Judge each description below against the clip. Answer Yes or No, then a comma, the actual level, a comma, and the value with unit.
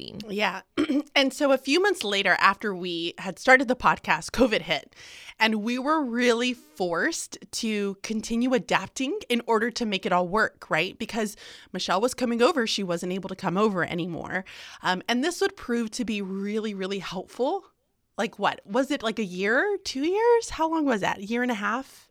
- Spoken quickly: No, average, 195 wpm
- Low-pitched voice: No, high, 225 Hz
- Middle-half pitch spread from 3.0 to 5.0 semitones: No, wide, 5.4 semitones